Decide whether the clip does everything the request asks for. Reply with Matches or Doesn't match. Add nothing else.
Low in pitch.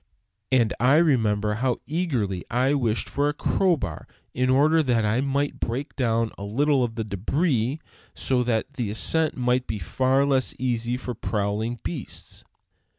Matches